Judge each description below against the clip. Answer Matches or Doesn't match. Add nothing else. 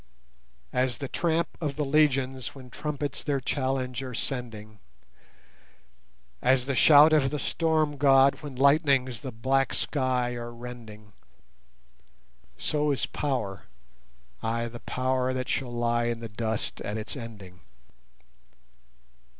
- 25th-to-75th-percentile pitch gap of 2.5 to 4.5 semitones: Matches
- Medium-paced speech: Doesn't match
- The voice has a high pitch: Doesn't match